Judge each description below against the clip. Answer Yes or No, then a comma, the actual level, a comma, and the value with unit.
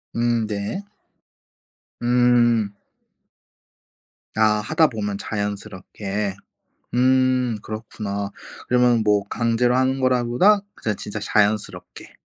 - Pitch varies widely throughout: No, average, 3.1 semitones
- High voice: No, low, 115 Hz